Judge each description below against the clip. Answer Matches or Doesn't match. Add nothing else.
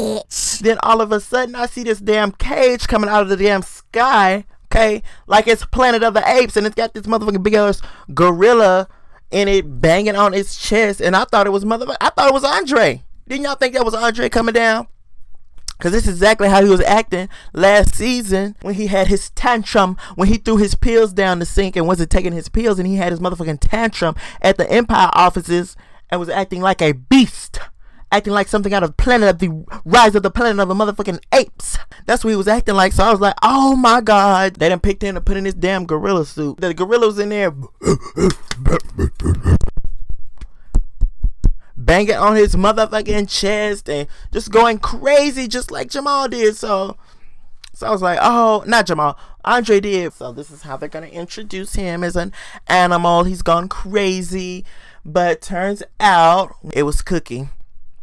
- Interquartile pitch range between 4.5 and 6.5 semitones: Doesn't match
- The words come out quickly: Doesn't match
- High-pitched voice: Matches